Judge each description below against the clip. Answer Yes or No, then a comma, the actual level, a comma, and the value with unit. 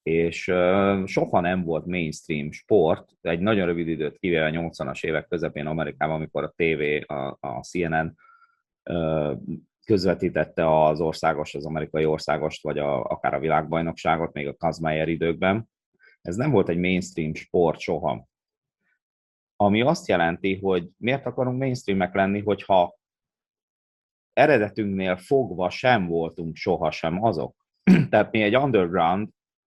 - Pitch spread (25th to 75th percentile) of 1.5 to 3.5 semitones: No, average, 4.3 semitones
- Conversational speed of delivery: Yes, average, 135 wpm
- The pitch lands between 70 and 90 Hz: Yes, very low, 85 Hz